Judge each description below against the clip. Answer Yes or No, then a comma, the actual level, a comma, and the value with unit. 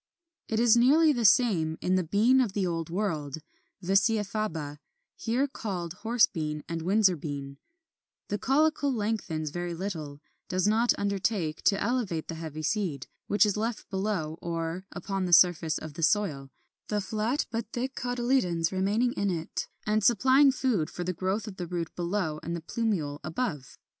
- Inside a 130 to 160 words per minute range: No, average, 170 wpm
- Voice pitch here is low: No, high, 195 Hz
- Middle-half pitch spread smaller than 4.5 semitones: No, wide, 5.4 semitones